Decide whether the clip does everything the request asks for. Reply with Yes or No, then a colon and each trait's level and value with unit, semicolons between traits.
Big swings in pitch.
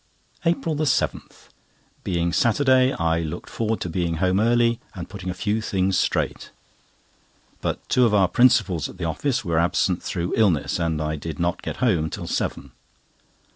Yes: wide, 5.7 semitones